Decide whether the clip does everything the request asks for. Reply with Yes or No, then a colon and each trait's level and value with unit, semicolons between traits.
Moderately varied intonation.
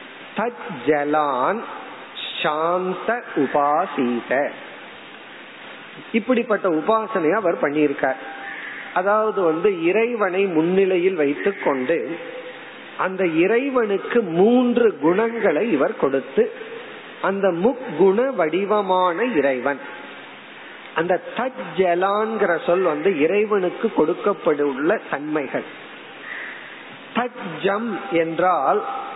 No: wide, 5.7 semitones